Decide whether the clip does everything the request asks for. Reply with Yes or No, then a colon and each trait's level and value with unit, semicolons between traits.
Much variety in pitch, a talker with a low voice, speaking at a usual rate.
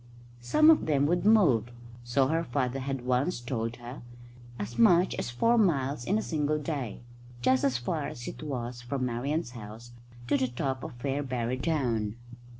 No: average, 3.8 semitones; low, 130 Hz; average, 170 wpm